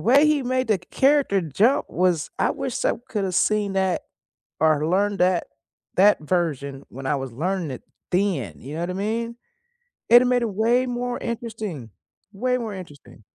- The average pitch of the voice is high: Yes, high, 195 Hz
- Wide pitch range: Yes, wide, 6.3 semitones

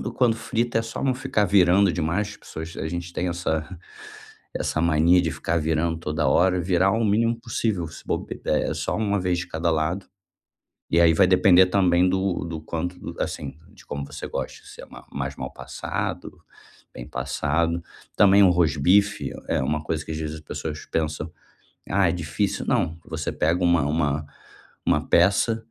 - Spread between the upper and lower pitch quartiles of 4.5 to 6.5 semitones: No, average, 3.4 semitones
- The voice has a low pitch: Yes, very low, 85 Hz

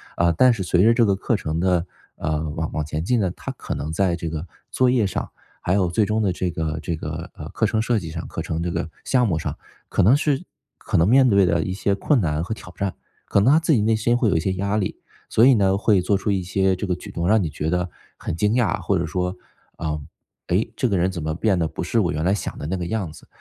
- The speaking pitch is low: Yes, very low, 95 Hz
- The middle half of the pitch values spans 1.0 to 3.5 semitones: No, average, 4.4 semitones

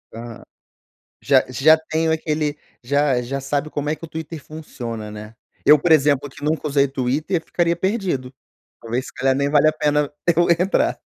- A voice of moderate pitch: Yes, medium, 145 Hz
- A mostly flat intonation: No, average, 3.2 semitones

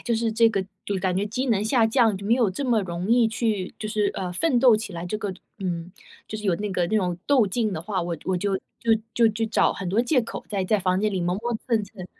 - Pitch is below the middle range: No, high, 210 Hz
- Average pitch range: Yes, average, 3.4 semitones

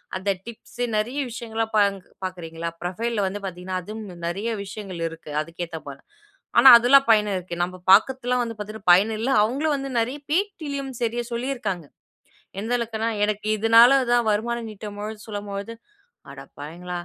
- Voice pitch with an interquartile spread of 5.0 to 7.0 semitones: No, average, 4.2 semitones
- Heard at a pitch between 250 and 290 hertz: No, high, 215 Hz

